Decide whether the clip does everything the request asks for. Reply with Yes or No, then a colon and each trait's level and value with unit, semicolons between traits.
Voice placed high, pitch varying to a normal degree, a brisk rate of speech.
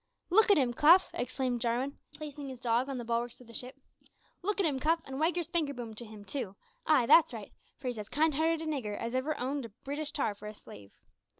Yes: very high, 265 Hz; average, 4.7 semitones; fast, 240 wpm